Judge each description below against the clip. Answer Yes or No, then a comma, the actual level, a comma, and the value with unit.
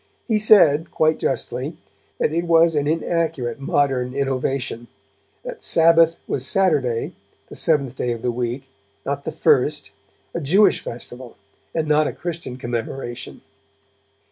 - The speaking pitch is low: No, medium, 145 Hz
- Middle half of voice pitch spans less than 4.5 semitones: No, average, 4.9 semitones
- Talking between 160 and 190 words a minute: No, slow, 135 wpm